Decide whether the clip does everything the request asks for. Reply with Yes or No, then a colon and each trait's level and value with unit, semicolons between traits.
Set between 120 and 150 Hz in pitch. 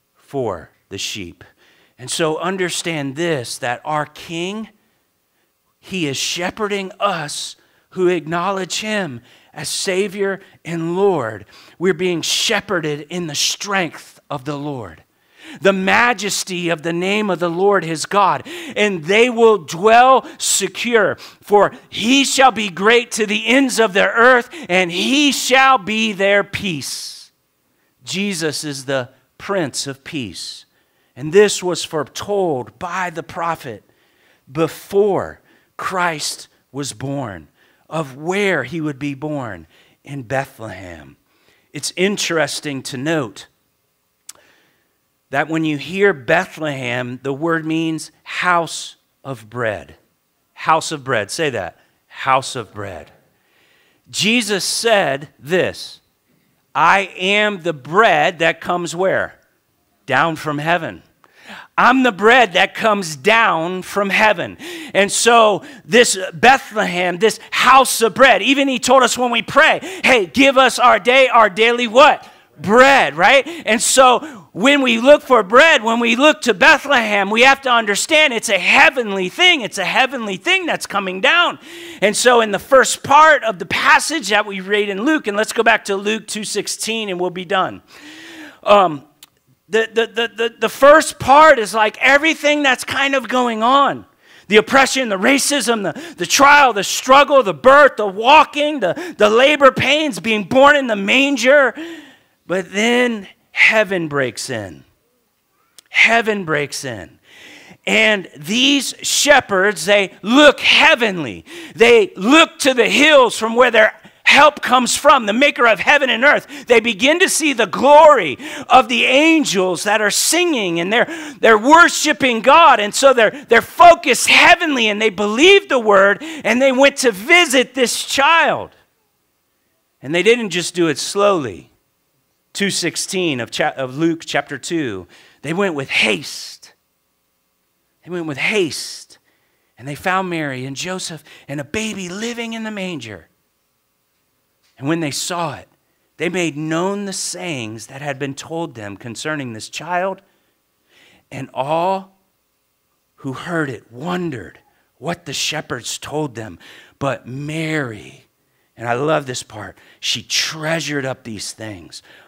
No: high, 195 Hz